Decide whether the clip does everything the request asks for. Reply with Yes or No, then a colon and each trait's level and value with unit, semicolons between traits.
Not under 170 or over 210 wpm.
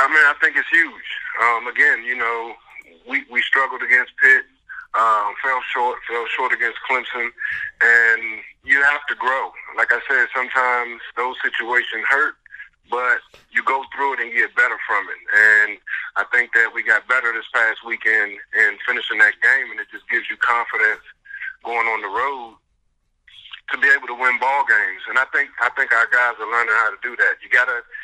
Yes: average, 195 wpm